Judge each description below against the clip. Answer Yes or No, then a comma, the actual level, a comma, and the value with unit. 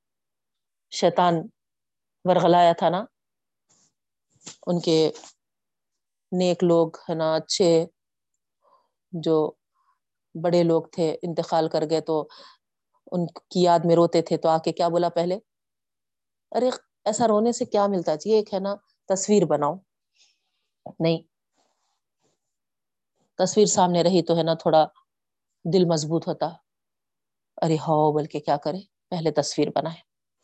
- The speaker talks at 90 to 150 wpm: Yes, average, 125 wpm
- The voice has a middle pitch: Yes, medium, 170 Hz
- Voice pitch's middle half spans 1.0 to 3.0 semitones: Yes, narrow, 2.5 semitones